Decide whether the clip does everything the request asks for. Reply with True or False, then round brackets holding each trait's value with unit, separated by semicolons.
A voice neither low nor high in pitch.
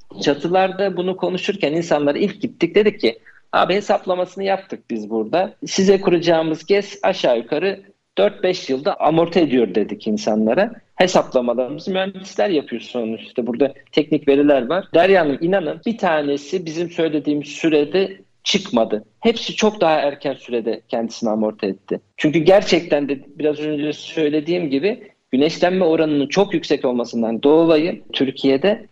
True (155 Hz)